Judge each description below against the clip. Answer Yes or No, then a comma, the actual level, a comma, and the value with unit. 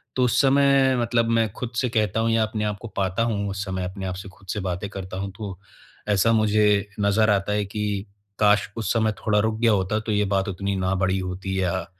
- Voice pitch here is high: No, low, 105 Hz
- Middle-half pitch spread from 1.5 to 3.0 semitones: Yes, narrow, 2.5 semitones